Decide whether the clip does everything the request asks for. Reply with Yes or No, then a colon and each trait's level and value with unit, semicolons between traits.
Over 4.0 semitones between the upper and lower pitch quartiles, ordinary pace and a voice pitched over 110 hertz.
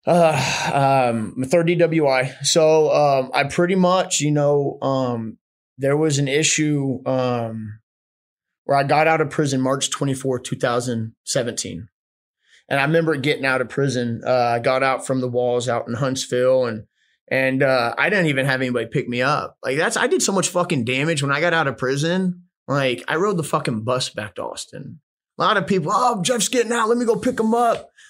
Yes: average, 4.6 semitones; average, 190 wpm; medium, 140 Hz